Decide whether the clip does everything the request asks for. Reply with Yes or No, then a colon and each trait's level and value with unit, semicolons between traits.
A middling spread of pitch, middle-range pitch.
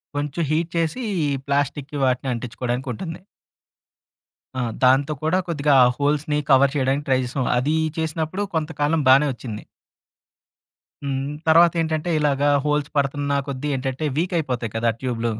Yes: average, 3.0 semitones; medium, 145 Hz